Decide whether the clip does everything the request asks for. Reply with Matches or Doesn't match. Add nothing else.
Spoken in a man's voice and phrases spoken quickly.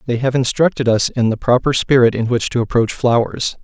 Matches